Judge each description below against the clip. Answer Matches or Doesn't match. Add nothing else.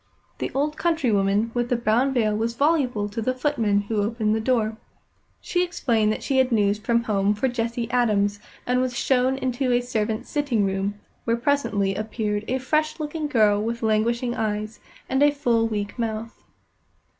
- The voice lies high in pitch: Matches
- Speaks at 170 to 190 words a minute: Matches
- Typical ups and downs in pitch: Matches